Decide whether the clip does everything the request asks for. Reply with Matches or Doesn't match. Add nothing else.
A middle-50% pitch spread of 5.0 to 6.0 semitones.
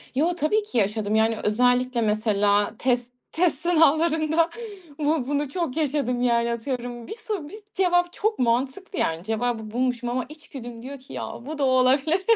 Matches